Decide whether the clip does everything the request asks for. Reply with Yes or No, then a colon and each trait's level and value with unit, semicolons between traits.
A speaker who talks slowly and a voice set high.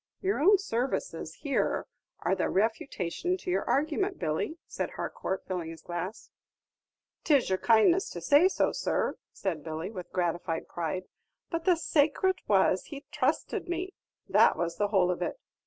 No: average, 155 wpm; high, 225 Hz